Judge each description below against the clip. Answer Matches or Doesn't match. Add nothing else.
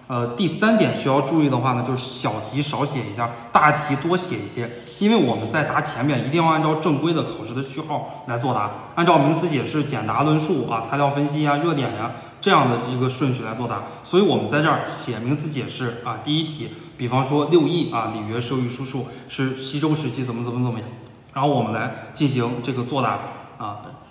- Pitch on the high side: Doesn't match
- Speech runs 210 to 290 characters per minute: Doesn't match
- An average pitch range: Matches